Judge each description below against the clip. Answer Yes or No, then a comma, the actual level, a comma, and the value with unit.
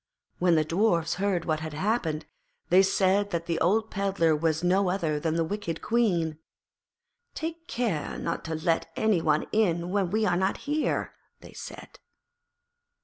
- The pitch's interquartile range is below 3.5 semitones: No, average, 3.8 semitones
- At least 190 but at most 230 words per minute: No, average, 160 wpm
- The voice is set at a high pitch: No, medium, 175 Hz